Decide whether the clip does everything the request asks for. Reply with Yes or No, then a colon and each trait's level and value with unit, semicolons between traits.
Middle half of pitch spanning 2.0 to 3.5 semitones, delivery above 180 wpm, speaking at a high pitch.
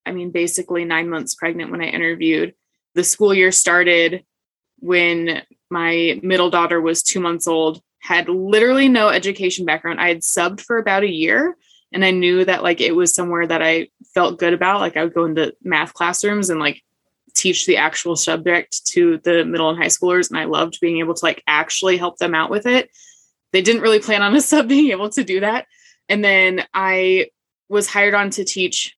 No: average, 3.2 semitones; fast, 205 wpm; medium, 180 Hz